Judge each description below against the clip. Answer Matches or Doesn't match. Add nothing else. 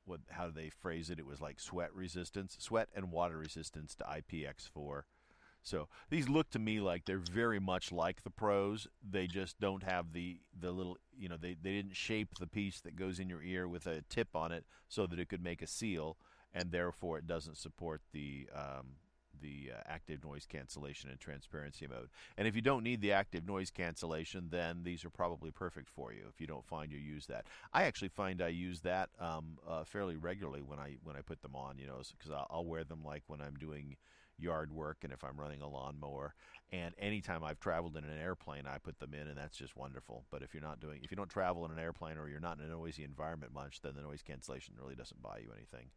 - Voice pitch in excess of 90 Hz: Doesn't match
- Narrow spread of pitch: Doesn't match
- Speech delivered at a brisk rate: Matches